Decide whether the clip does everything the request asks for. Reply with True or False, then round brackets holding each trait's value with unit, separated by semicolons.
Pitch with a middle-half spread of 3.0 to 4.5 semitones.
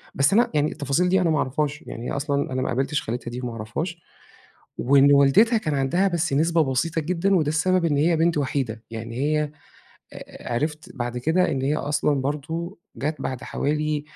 True (3.5 semitones)